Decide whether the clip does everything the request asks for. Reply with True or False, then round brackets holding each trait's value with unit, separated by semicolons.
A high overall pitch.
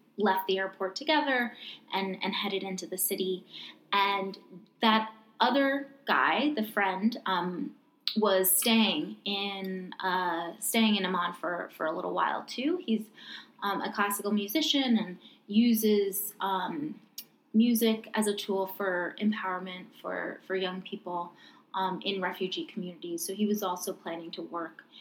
True (200 Hz)